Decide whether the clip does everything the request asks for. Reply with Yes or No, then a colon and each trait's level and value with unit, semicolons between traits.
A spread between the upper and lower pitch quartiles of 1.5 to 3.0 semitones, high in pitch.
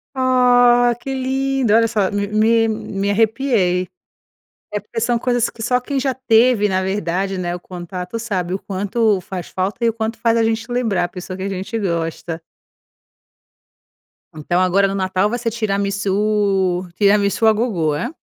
No: average, 3.8 semitones; high, 210 Hz